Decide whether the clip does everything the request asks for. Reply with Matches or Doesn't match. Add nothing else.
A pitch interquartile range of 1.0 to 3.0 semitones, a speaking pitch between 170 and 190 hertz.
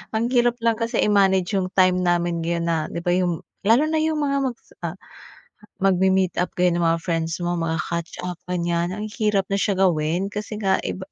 Doesn't match